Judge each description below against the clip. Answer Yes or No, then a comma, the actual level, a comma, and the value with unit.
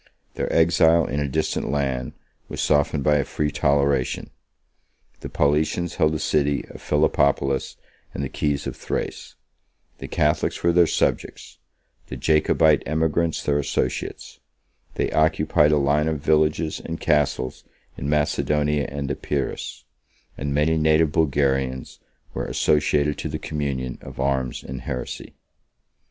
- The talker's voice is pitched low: Yes, very low, 75 Hz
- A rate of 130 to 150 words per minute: Yes, slow, 135 wpm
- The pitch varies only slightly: Yes, narrow, 1.8 semitones